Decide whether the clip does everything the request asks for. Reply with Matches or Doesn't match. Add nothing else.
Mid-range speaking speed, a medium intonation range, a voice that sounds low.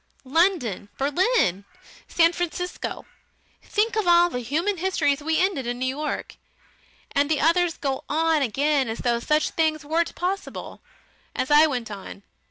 Doesn't match